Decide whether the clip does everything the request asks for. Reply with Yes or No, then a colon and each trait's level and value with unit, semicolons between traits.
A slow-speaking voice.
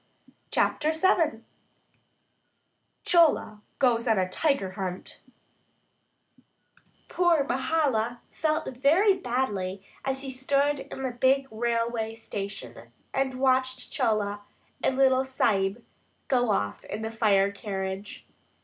Yes: slow, 110 wpm